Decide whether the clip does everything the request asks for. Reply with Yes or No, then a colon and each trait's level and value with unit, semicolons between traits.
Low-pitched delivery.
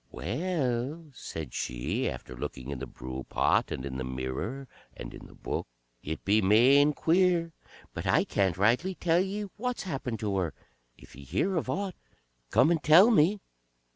Yes: low, 125 Hz